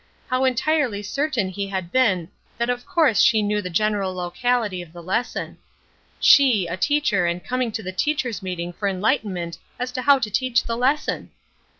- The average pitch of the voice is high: Yes, high, 215 Hz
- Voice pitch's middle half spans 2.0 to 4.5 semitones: No, wide, 5.4 semitones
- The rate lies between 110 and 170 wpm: No, average, 180 wpm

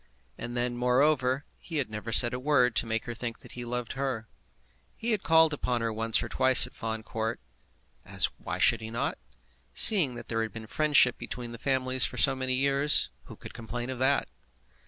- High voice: No, low, 125 Hz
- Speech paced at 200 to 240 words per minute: Yes, fast, 205 wpm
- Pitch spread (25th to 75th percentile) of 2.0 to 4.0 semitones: Yes, average, 2.7 semitones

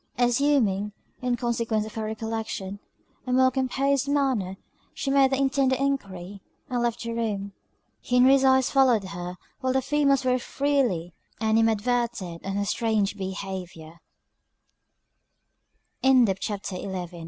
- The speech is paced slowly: Yes, slow, 115 wpm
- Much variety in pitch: No, average, 4.7 semitones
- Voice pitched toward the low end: No, high, 235 Hz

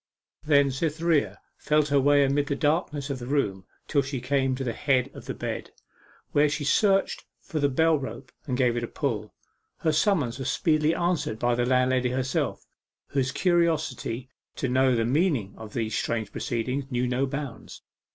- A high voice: No, low, 135 Hz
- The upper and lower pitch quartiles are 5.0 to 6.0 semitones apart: No, average, 3.3 semitones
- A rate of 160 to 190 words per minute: Yes, average, 180 wpm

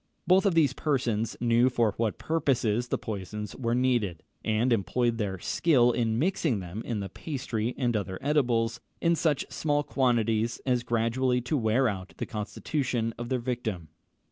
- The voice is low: Yes, low, 120 Hz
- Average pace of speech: Yes, average, 160 wpm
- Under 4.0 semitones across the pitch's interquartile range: Yes, average, 3.1 semitones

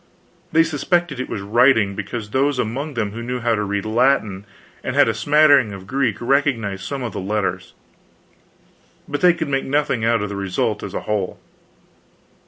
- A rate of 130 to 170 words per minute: No, average, 185 wpm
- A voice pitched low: Yes, low, 120 Hz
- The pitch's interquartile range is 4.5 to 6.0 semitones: Yes, average, 5.2 semitones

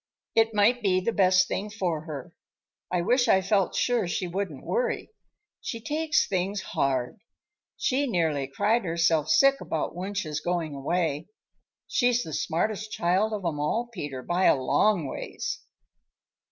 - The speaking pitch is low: No, medium, 185 Hz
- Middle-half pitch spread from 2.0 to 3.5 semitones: No, wide, 5.4 semitones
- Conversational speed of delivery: Yes, average, 150 wpm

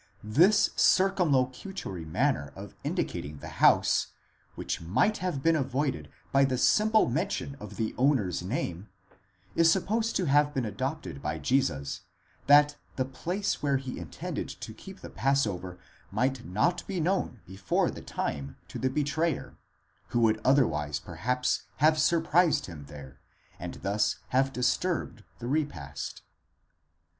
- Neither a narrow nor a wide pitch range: No, wide, 7.4 semitones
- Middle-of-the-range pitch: No, low, 130 Hz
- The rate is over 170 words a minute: No, average, 140 wpm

